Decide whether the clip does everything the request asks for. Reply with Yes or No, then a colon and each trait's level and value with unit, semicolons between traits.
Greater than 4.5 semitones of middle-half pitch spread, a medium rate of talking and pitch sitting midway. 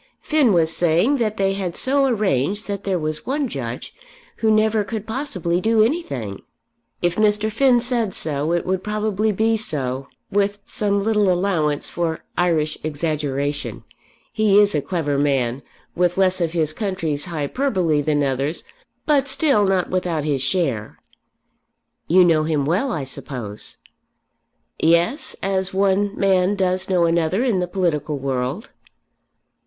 Yes: wide, 5.5 semitones; average, 145 wpm; medium, 180 Hz